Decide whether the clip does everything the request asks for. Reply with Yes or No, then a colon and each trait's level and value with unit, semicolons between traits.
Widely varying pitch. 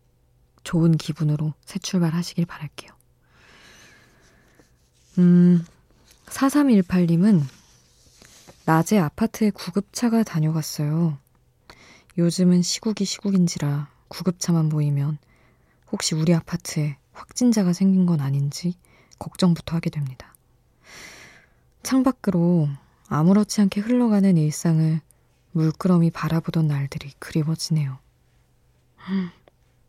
No: average, 3.8 semitones